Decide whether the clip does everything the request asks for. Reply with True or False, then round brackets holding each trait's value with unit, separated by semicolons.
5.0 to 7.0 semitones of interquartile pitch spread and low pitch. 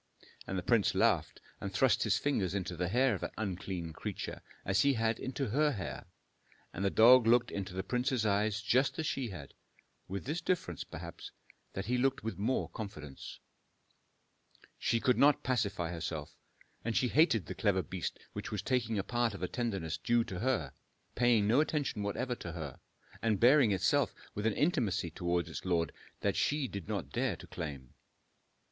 True (5.3 semitones; 105 Hz)